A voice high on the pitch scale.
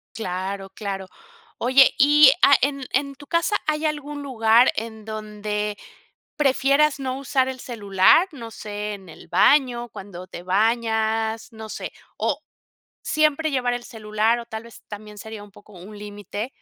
Yes: high, 225 Hz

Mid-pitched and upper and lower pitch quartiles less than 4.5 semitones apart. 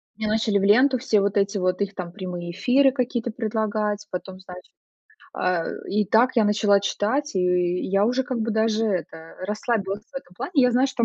No: high, 210 Hz; average, 3.2 semitones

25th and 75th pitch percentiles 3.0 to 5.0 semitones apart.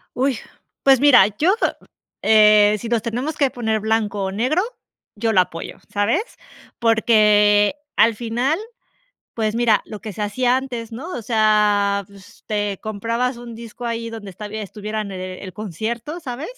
No: narrow, 2.6 semitones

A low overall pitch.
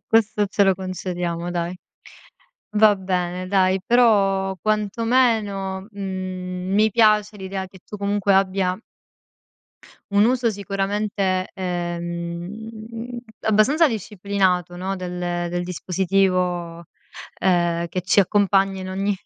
No: high, 195 Hz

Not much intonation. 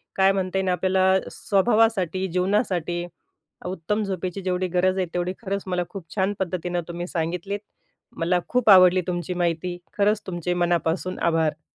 Yes: narrow, 1.6 semitones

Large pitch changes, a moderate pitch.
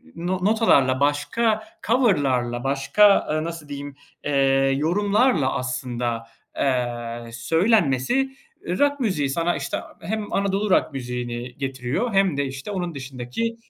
Yes: wide, 7.7 semitones; medium, 145 Hz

